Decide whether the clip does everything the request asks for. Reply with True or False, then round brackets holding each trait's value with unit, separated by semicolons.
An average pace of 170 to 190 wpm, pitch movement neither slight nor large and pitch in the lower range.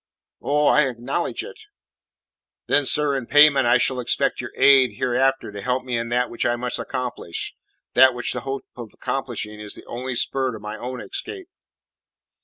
False (180 wpm; 2.3 semitones; 125 Hz)